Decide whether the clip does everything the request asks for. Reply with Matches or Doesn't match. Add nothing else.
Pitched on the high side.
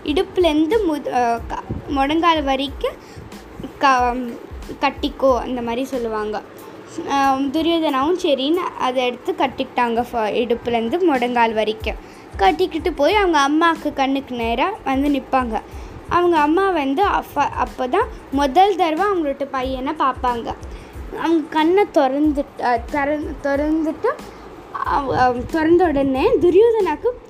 Matches